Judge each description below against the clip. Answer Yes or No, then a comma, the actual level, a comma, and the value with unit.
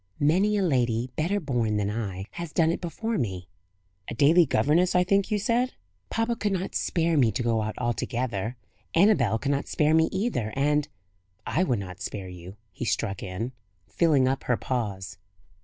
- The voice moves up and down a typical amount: No, wide, 7.9 semitones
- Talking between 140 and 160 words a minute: No, average, 185 wpm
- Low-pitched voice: Yes, low, 130 Hz